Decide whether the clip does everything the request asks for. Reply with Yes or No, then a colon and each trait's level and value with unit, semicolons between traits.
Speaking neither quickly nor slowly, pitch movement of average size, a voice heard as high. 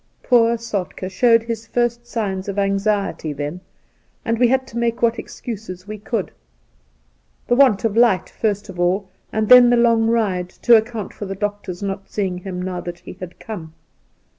Yes: average, 190 wpm; average, 3.9 semitones; high, 205 Hz